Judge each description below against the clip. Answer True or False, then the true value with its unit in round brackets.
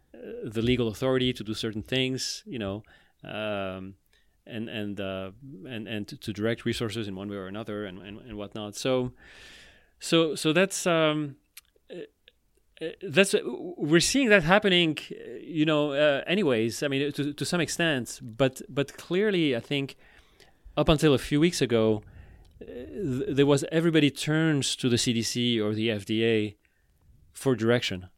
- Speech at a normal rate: True (150 wpm)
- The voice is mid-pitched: False (125 Hz)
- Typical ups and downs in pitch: False (5.9 semitones)